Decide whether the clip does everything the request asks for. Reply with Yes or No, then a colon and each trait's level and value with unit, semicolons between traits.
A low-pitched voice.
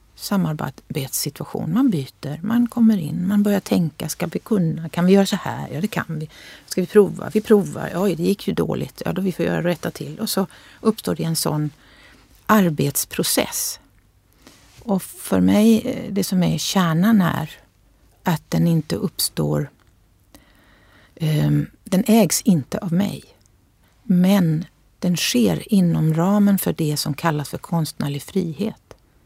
No: medium, 175 Hz